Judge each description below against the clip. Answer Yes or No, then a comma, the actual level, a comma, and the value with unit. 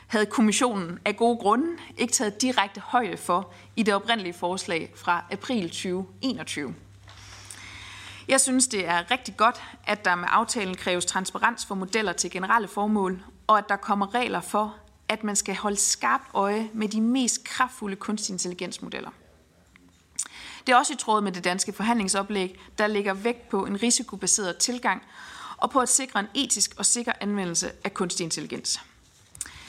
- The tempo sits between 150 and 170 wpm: Yes, average, 160 wpm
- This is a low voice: No, high, 205 Hz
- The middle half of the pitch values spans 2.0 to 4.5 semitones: Yes, average, 4.2 semitones